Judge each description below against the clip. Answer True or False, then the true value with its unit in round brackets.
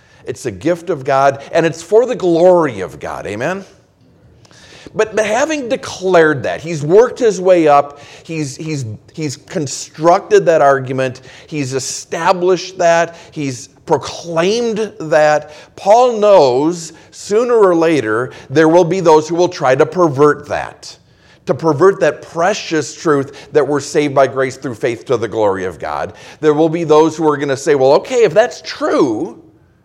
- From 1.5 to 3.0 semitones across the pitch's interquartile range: False (4.2 semitones)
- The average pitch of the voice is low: False (160 Hz)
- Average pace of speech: True (165 wpm)